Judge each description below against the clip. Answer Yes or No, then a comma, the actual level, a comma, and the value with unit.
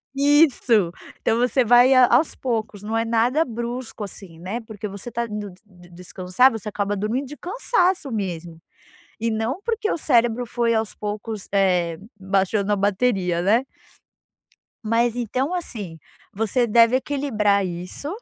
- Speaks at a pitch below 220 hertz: No, high, 225 Hz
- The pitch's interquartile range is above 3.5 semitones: Yes, average, 4.0 semitones